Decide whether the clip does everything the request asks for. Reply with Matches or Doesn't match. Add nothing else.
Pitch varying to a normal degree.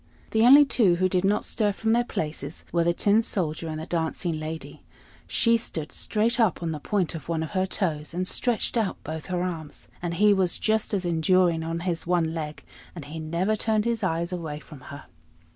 Matches